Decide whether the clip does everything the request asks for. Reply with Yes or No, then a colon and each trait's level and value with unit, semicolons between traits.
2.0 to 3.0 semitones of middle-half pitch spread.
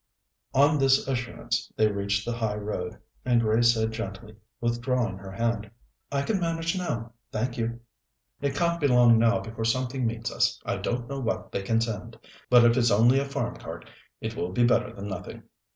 Yes: narrow, 2.6 semitones